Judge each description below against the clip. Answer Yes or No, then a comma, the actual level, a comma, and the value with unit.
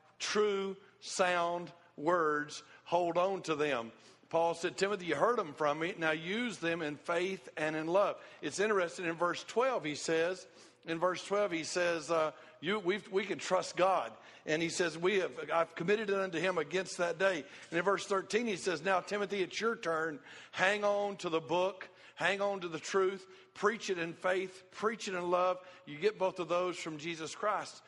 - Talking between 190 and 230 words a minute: Yes, average, 200 wpm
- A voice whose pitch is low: No, medium, 180 Hz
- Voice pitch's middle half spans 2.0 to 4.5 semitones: Yes, average, 2.8 semitones